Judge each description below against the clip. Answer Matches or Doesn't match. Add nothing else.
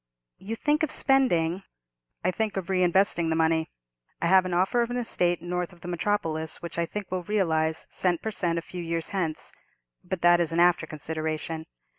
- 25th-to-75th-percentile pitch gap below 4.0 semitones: Matches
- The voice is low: Doesn't match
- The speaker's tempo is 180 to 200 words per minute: Matches